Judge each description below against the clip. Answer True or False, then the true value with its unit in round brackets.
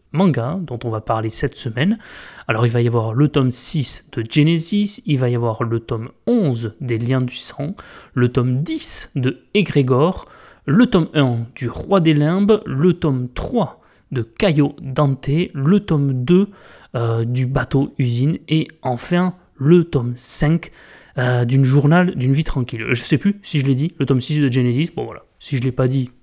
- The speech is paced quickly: False (190 wpm)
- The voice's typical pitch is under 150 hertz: True (140 Hz)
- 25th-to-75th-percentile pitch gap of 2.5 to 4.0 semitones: False (4.5 semitones)